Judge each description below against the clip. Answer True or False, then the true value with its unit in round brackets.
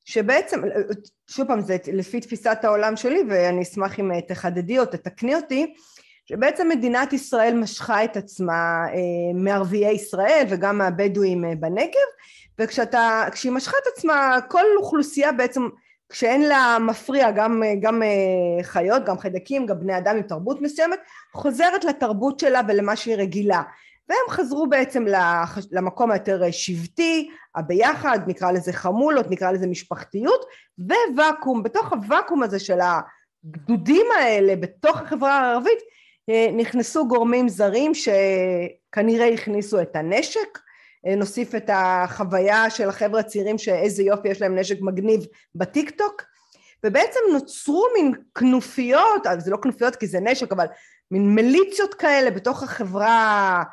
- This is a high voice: True (225 Hz)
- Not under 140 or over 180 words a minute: False (125 wpm)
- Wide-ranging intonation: True (6.2 semitones)